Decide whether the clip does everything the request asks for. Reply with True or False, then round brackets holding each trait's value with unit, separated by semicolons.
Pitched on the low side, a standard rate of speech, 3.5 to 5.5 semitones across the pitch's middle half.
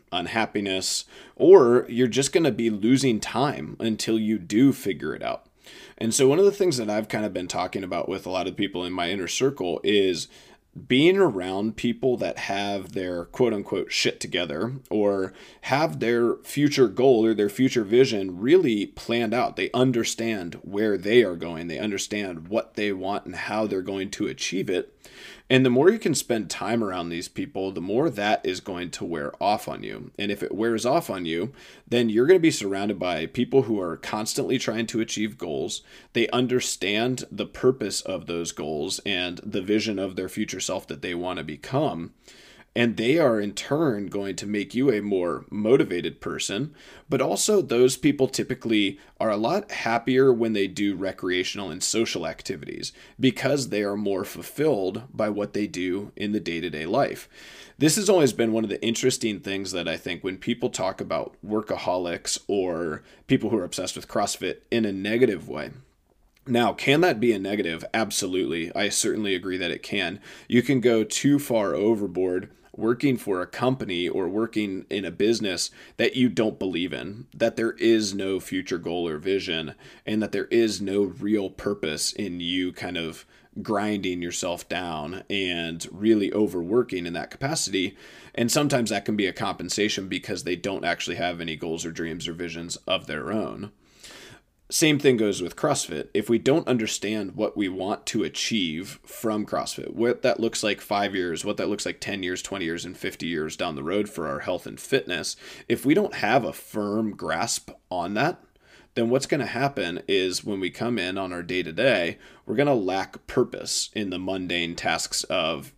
True (105 Hz; 190 wpm; 4.0 semitones)